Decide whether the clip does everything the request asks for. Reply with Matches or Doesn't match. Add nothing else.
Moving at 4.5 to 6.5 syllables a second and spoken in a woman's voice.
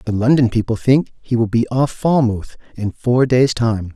Doesn't match